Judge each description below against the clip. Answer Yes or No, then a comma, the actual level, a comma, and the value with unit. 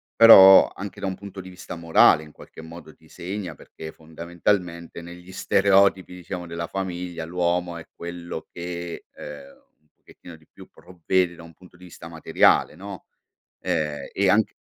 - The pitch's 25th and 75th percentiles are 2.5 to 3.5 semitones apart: No, narrow, 2.0 semitones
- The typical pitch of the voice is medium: No, very low, 85 Hz